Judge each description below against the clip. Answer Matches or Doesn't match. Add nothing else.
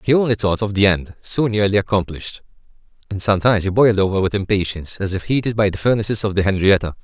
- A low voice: Matches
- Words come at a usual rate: Doesn't match